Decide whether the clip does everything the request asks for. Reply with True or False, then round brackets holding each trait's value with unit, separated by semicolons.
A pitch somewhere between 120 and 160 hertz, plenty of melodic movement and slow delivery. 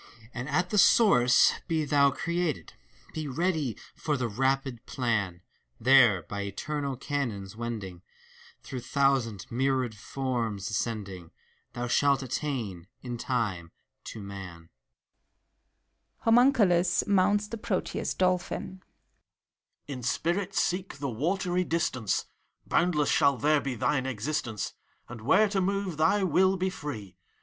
True (135 Hz; 7.2 semitones; 125 wpm)